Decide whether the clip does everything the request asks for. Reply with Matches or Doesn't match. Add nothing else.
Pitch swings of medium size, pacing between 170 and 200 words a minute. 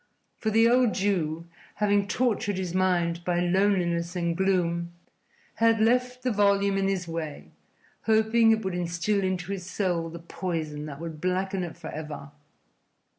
Doesn't match